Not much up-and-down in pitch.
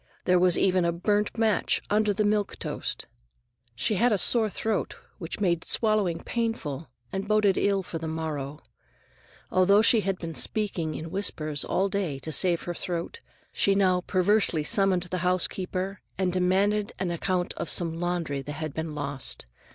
No: average, 3.5 semitones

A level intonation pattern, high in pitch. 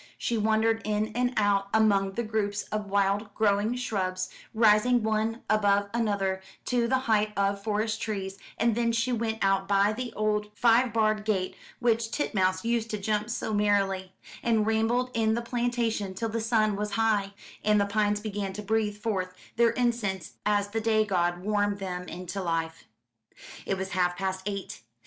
Yes: narrow, 2.3 semitones; high, 210 Hz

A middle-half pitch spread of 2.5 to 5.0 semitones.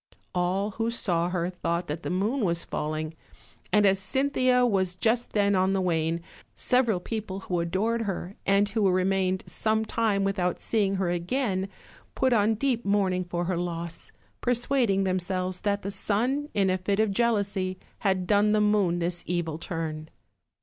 Yes: average, 3.3 semitones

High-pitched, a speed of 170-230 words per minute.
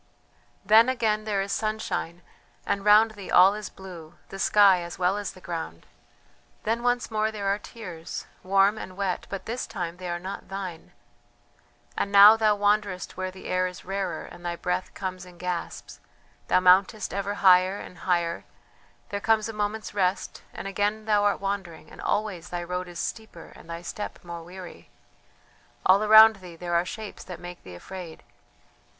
Yes: high, 195 Hz; average, 180 wpm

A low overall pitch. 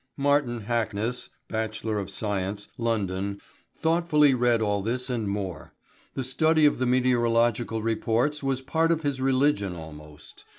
Yes: low, 115 Hz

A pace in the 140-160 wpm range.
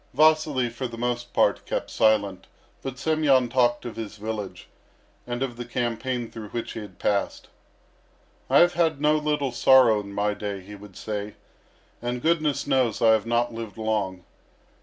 No: average, 170 wpm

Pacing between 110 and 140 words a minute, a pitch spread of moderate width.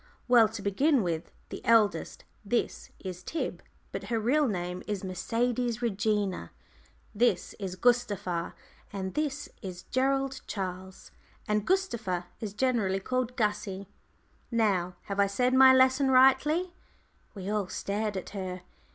Yes: slow, 135 wpm; average, 5.0 semitones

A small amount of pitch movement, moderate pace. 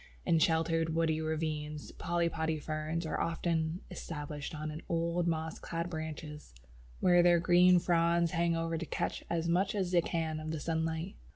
Yes: narrow, 1.3 semitones; average, 160 wpm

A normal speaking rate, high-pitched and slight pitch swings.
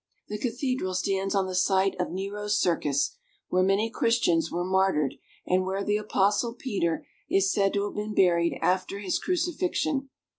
Yes: average, 160 wpm; high, 195 Hz; narrow, 2.3 semitones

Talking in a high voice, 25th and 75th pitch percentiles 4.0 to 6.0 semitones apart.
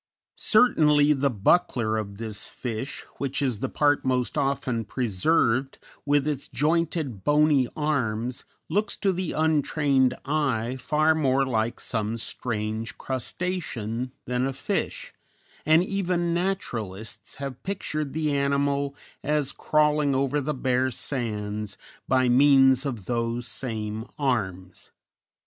No: low, 135 Hz; average, 4.4 semitones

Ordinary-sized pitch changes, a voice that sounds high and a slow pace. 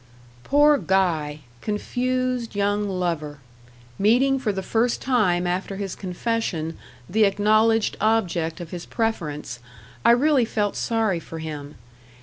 Yes: average, 4.7 semitones; high, 205 Hz; slow, 125 wpm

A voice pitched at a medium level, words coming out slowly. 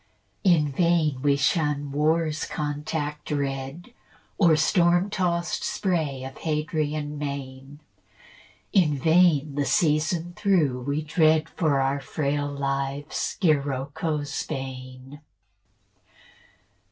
Yes: medium, 150 Hz; slow, 95 wpm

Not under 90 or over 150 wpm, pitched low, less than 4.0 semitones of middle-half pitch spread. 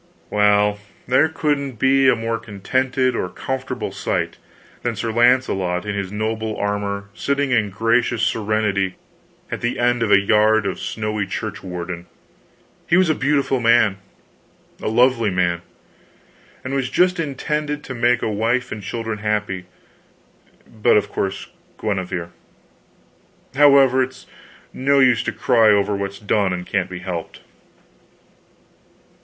No: average, 140 wpm; low, 110 Hz; average, 4.4 semitones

